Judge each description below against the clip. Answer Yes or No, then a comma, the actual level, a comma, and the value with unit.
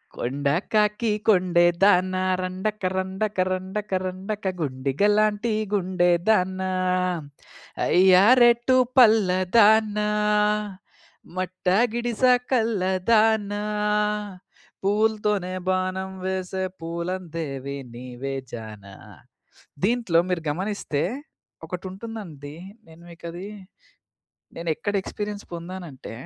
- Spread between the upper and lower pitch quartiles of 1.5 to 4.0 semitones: Yes, average, 3.6 semitones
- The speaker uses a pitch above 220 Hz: No, medium, 185 Hz